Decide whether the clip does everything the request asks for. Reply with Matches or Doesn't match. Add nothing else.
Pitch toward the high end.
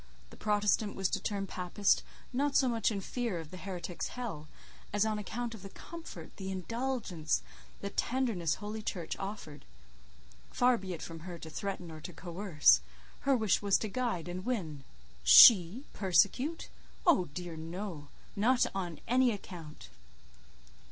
Matches